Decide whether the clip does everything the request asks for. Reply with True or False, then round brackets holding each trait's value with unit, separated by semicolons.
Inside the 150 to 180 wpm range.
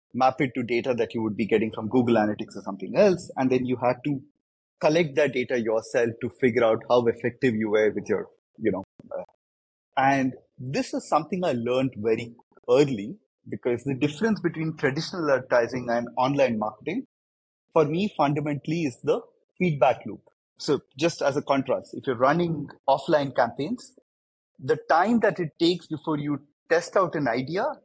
True (170 wpm)